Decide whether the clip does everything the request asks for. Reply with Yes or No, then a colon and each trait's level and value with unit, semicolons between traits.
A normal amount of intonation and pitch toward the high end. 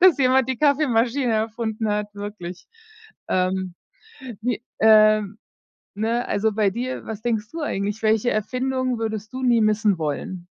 Yes: average, 3.0 semitones; high, 220 Hz